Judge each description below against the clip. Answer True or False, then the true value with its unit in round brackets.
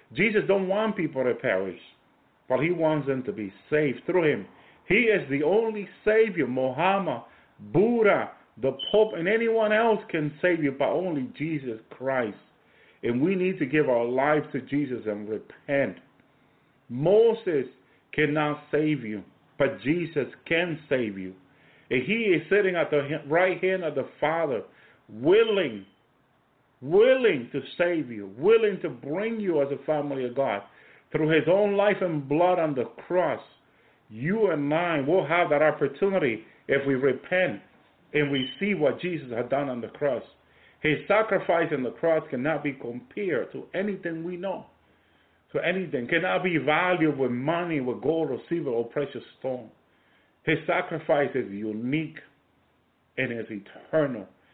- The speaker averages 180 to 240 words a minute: False (155 wpm)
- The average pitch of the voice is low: False (155 Hz)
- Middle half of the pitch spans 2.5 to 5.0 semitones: False (5.4 semitones)